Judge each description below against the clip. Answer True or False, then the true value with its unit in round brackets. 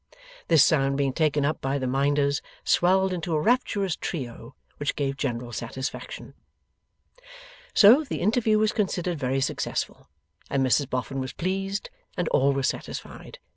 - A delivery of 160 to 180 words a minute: False (145 wpm)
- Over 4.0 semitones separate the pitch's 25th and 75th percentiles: True (5.6 semitones)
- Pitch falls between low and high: True (145 Hz)